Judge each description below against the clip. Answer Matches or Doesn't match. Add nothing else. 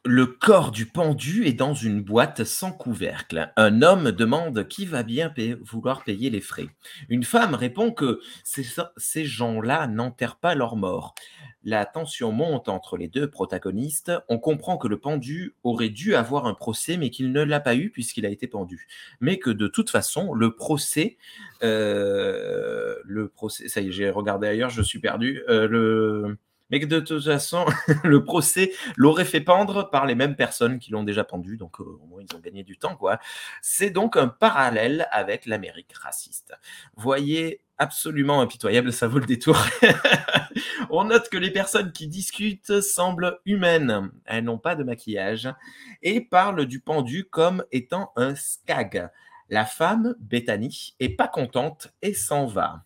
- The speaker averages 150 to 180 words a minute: Matches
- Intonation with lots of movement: Matches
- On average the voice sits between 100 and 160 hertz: Matches